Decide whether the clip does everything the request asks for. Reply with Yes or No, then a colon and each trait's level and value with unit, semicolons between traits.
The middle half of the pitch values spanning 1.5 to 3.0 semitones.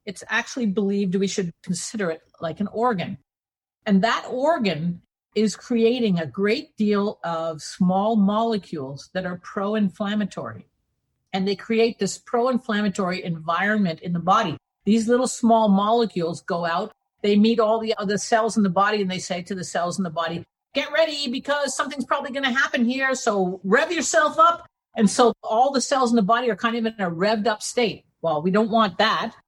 No: average, 3.9 semitones